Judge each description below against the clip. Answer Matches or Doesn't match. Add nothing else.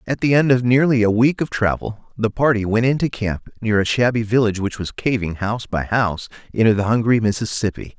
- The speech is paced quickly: Matches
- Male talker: Matches